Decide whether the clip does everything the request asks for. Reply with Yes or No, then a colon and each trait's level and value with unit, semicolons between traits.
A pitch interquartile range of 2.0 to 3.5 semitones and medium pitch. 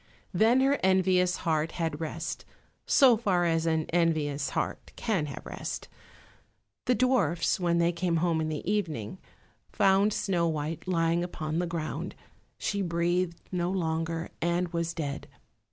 Yes: narrow, 2.4 semitones; medium, 170 Hz